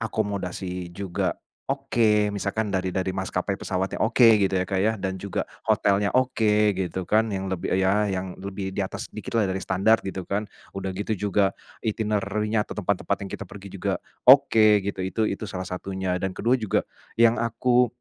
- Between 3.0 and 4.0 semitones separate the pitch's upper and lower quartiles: No, narrow, 2.5 semitones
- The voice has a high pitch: No, low, 100 Hz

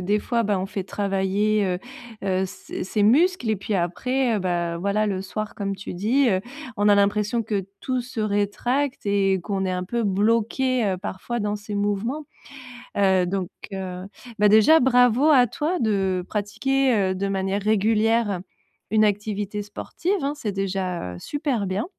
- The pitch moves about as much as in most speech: Yes, average, 3.2 semitones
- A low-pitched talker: No, high, 205 Hz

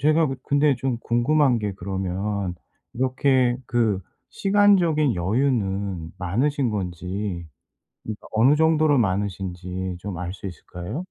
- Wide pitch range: Yes, wide, 6.9 semitones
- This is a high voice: No, low, 105 Hz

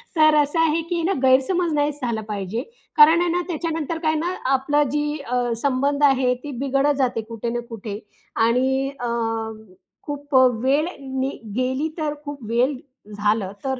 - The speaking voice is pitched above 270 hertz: Yes, very high, 280 Hz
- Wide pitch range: No, average, 3.7 semitones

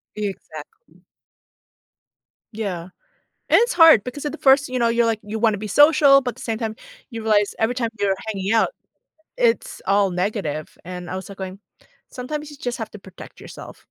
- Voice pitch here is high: Yes, high, 220 Hz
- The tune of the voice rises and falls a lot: No, average, 4.9 semitones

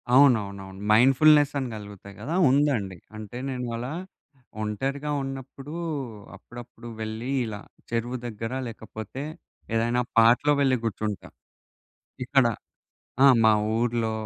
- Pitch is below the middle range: Yes, low, 120 Hz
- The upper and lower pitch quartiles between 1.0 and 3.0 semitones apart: No, average, 3.7 semitones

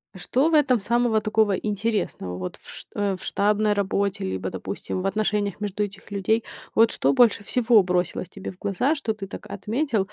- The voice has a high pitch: Yes, high, 205 Hz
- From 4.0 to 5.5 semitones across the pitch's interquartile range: No, average, 2.7 semitones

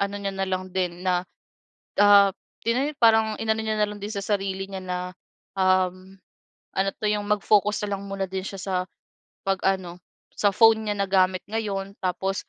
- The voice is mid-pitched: No, high, 195 Hz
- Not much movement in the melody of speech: Yes, narrow, 1.7 semitones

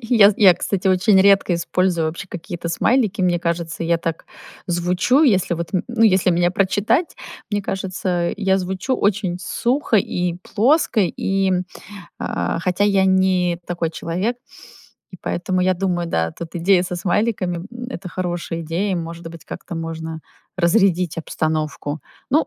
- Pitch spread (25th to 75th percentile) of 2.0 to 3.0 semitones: Yes, average, 2.7 semitones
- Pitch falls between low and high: Yes, medium, 180 Hz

